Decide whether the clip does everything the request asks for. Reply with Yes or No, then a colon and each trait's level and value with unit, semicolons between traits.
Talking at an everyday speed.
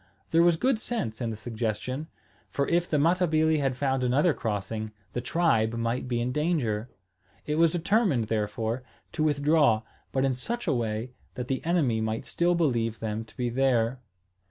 Yes: average, 175 wpm